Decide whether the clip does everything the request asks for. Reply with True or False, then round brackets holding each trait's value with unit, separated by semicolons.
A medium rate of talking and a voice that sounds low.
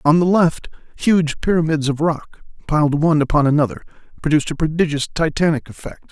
False (155 wpm; 155 Hz)